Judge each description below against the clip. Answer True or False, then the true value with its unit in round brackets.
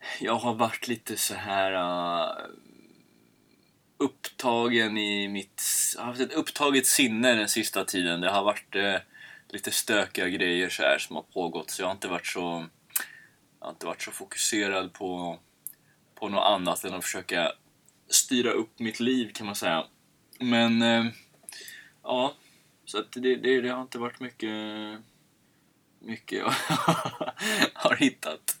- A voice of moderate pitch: False (115 Hz)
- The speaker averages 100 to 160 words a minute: True (155 wpm)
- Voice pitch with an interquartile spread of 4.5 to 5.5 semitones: False (4.0 semitones)